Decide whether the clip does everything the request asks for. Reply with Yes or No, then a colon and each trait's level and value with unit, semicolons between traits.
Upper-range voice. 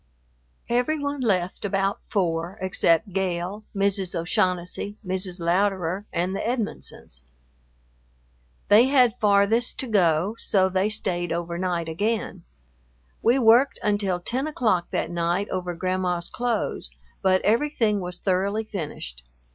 Yes: high, 195 Hz